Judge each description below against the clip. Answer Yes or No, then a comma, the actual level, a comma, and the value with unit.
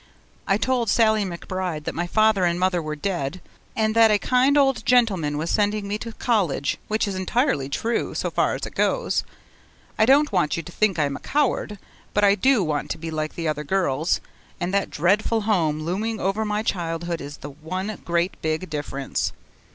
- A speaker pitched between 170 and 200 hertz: Yes, medium, 185 Hz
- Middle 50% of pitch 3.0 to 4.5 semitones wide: No, average, 5.3 semitones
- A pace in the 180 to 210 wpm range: Yes, average, 200 wpm